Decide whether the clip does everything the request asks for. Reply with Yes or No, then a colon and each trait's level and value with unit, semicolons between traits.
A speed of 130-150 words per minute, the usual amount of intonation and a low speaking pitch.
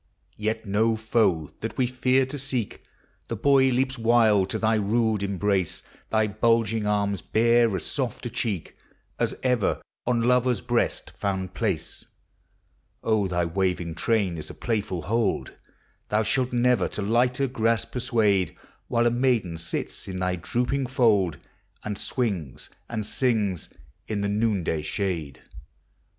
Yes: average, 145 wpm; average, 3.7 semitones; low, 110 Hz